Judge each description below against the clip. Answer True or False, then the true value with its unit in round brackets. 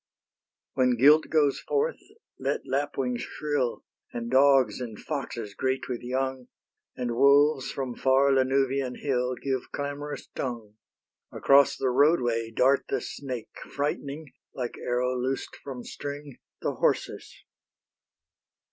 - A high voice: False (130 Hz)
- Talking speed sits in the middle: False (120 wpm)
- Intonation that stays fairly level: True (2.3 semitones)